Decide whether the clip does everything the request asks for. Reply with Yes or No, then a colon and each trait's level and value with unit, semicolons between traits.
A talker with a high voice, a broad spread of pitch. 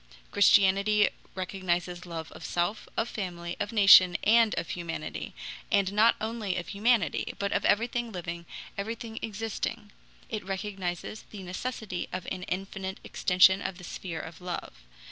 No: high, 195 Hz; average, 3.2 semitones